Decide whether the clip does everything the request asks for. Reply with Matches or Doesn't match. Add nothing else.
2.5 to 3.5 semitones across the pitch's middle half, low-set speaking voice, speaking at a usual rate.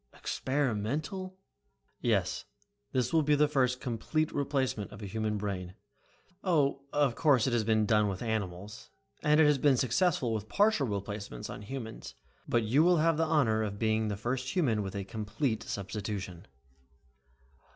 Doesn't match